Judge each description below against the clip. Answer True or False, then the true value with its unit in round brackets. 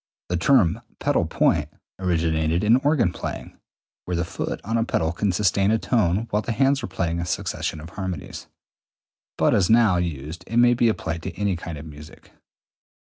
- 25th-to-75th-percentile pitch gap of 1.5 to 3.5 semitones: False (5.3 semitones)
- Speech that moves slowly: False (185 wpm)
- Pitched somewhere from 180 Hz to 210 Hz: False (90 Hz)